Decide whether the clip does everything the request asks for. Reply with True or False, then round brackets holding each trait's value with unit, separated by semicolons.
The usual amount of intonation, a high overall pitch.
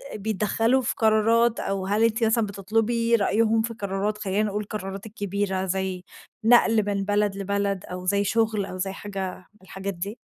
False (2.3 semitones; 205 Hz)